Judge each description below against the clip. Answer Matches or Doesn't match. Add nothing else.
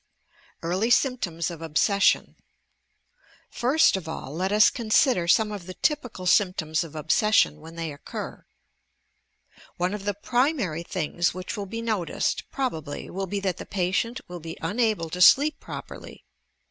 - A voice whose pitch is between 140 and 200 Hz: Matches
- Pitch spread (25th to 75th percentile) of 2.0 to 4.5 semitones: Doesn't match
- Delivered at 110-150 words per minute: Matches